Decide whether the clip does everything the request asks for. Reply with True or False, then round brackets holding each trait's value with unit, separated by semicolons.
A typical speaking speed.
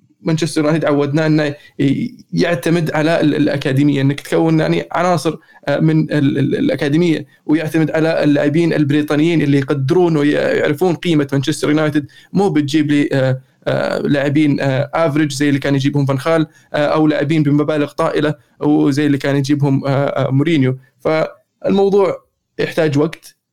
True (115 wpm)